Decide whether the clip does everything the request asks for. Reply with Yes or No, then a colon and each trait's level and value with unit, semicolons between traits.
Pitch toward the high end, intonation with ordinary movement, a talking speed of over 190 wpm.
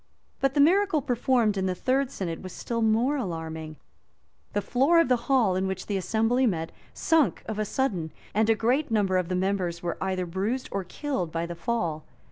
No: high, 210 Hz; wide, 5.9 semitones; fast, 205 wpm